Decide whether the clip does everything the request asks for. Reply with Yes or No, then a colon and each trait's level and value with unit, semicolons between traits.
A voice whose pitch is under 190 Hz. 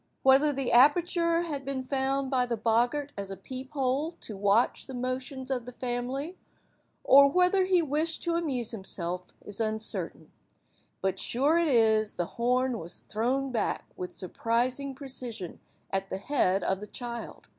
No: very high, 255 Hz